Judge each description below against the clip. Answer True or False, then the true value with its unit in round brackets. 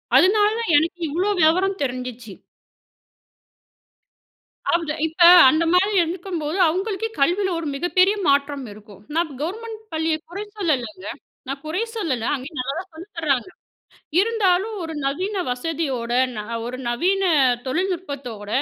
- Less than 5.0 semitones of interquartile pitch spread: False (5.5 semitones)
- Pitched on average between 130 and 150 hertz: False (330 Hz)